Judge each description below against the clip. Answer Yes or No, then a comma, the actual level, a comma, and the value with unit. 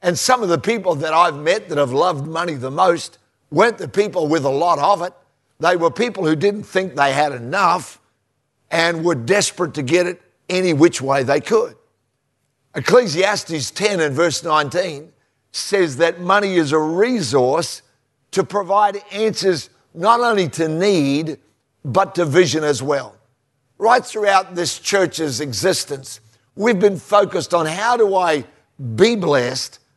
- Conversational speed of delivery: Yes, average, 160 wpm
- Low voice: No, medium, 170 Hz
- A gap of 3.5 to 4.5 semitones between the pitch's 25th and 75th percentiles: No, wide, 5.4 semitones